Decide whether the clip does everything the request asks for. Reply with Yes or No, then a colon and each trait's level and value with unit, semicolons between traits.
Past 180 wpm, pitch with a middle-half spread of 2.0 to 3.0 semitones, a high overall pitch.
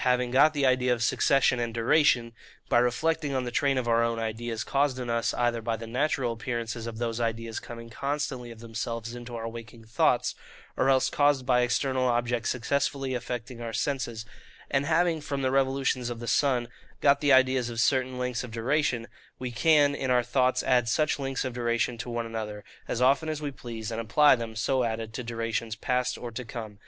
No: average, 200 wpm; narrow, 2.4 semitones; low, 120 Hz